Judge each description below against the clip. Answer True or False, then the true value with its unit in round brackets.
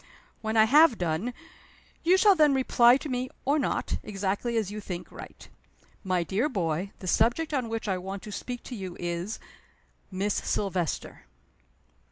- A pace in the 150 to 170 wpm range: True (165 wpm)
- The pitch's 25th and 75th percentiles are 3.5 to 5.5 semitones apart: True (5.1 semitones)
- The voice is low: False (215 Hz)